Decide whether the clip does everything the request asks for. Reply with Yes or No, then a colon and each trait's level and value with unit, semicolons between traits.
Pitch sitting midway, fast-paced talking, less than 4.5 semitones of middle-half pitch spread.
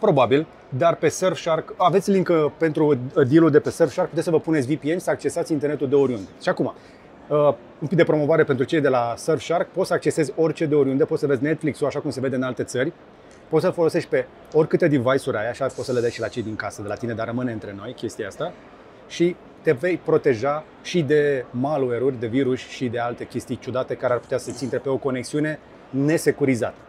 Yes: medium, 145 Hz; fast, 220 wpm; average, 3.9 semitones